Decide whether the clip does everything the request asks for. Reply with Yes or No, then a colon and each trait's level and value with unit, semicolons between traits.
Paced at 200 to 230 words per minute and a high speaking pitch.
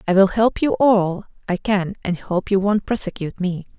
Yes: fast, 205 wpm; high, 195 Hz